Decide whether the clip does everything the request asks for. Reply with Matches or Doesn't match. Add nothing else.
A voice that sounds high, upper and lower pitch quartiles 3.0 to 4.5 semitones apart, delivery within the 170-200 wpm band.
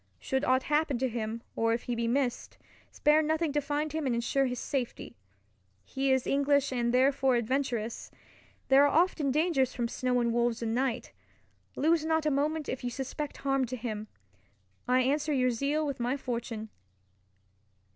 Matches